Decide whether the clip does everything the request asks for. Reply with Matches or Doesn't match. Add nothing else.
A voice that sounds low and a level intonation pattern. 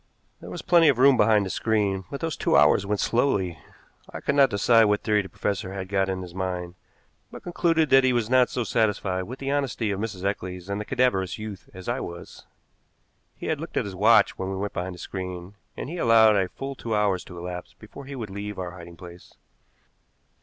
Doesn't match